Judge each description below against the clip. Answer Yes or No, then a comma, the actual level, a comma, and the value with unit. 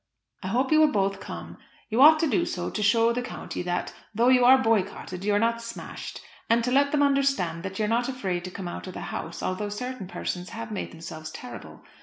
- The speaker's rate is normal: No, fast, 235 wpm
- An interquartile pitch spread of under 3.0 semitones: No, wide, 5.4 semitones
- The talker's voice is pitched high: Yes, high, 225 Hz